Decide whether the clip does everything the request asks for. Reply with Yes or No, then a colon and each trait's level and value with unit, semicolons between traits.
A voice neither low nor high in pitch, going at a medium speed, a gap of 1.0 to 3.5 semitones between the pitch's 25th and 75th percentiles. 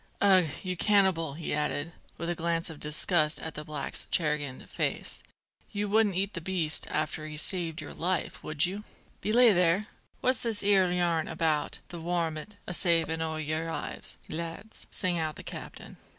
Yes: medium, 170 Hz; average, 175 wpm; average, 3.2 semitones